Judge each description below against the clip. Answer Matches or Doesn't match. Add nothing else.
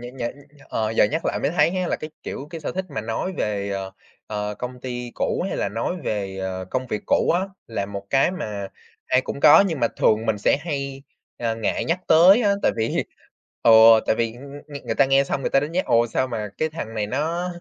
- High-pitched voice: Doesn't match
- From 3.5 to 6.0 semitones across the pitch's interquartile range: Matches